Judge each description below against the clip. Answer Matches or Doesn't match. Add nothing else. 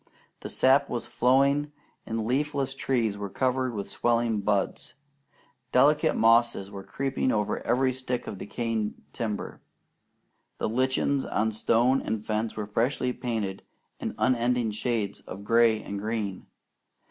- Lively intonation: Doesn't match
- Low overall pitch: Matches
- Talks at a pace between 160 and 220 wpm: Doesn't match